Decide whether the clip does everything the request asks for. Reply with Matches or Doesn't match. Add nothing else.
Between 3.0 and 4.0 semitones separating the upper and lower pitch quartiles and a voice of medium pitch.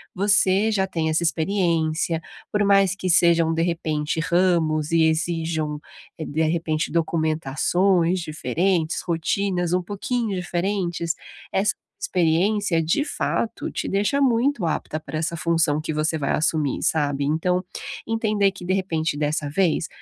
Matches